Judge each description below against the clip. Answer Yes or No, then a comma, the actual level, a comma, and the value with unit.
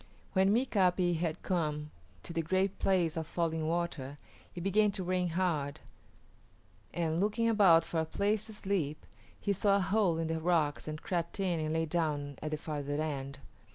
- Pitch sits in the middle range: Yes, medium, 170 Hz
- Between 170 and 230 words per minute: Yes, average, 180 wpm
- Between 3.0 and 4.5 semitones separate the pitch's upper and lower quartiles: Yes, average, 3.5 semitones